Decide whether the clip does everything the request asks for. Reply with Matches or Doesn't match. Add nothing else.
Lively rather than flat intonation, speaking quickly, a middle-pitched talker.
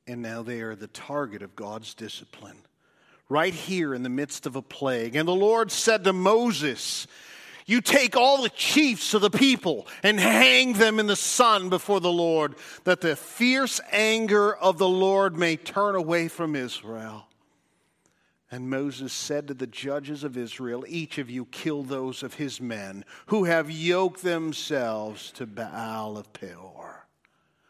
Doesn't match